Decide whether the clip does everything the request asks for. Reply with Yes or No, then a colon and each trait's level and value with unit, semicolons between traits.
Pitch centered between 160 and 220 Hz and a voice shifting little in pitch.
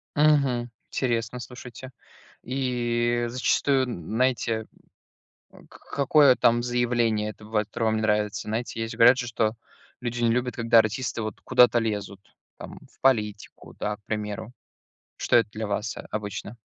No: low, 115 Hz; narrow, 2.3 semitones